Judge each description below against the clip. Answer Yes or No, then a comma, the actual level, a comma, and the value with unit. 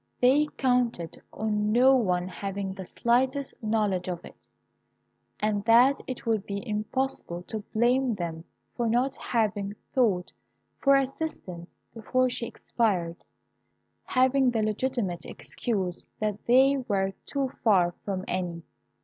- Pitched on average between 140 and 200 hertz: No, high, 220 Hz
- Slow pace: Yes, slow, 130 wpm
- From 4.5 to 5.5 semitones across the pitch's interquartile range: Yes, average, 4.9 semitones